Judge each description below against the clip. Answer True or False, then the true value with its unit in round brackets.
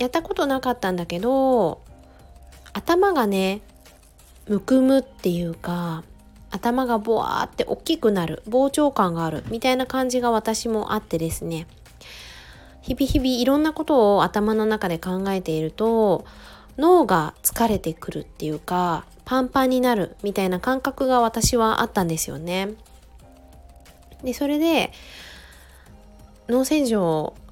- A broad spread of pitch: True (7.4 semitones)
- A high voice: True (215 Hz)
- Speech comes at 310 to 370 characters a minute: False (270 characters per minute)